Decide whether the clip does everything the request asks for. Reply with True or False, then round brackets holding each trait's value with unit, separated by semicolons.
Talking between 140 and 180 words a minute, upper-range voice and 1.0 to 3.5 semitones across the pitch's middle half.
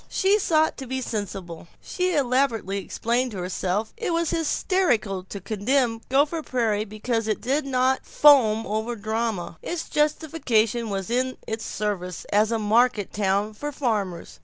False (160 wpm; 230 Hz; 4.8 semitones)